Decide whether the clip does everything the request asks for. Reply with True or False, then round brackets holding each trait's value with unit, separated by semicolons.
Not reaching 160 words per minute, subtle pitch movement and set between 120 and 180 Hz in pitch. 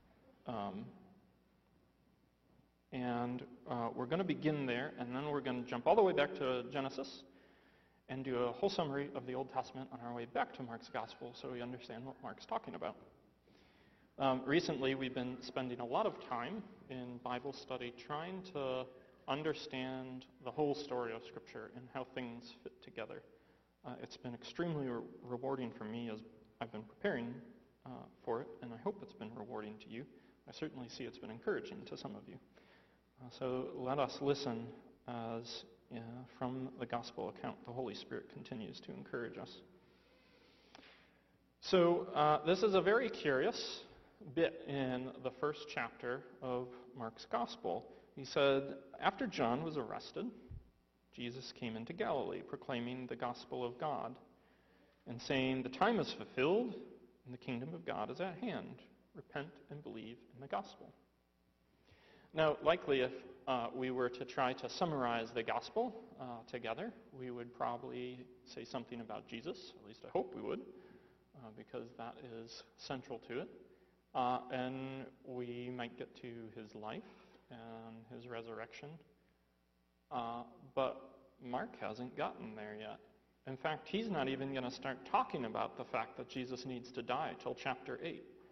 False (165 wpm; 2.2 semitones; 125 Hz)